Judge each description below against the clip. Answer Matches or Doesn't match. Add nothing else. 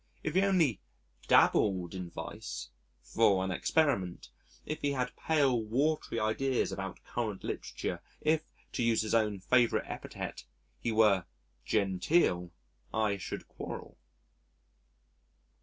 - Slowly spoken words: Matches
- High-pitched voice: Doesn't match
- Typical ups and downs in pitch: Doesn't match